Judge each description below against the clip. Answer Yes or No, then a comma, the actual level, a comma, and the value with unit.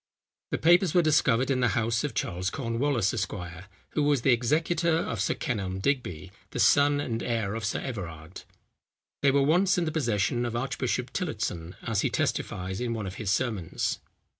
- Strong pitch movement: Yes, wide, 5.9 semitones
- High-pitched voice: No, low, 120 Hz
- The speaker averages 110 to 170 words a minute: No, average, 180 wpm